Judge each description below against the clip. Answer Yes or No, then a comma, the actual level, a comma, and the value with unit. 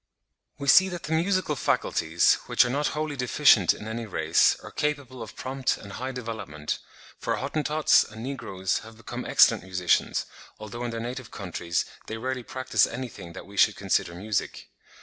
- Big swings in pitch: Yes, wide, 5.8 semitones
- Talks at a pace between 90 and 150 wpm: No, average, 170 wpm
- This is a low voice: Yes, low, 120 Hz